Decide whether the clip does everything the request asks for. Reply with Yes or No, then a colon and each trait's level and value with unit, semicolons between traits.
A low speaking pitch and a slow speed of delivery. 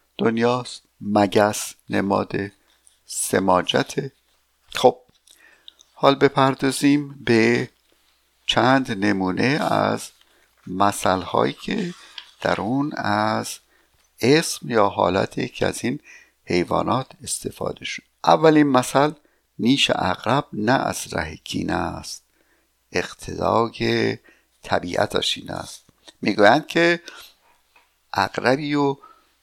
Yes: low, 120 Hz; slow, 90 wpm